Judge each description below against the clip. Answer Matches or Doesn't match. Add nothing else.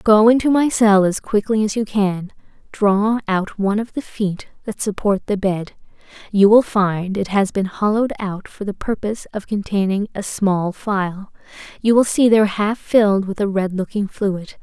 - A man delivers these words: Doesn't match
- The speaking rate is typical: Matches